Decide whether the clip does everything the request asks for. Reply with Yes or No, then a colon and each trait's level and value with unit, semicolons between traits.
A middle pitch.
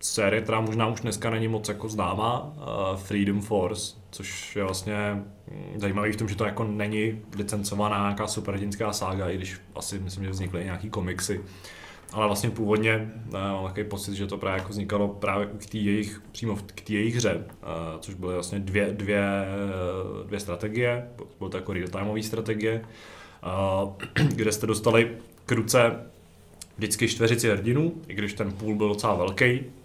No: low, 105 Hz